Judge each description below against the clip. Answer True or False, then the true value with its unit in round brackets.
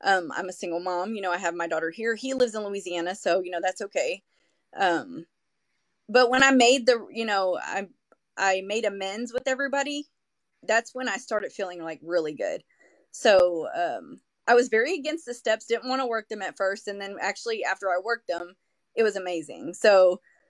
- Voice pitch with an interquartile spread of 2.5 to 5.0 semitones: False (5.4 semitones)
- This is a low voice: False (210 Hz)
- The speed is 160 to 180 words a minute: False (200 wpm)